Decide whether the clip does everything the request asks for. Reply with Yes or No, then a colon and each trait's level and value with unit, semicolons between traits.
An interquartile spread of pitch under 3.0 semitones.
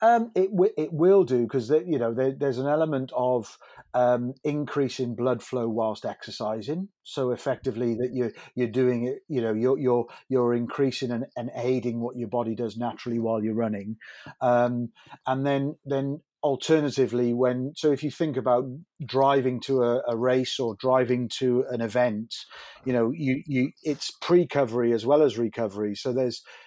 Yes: narrow, 2.6 semitones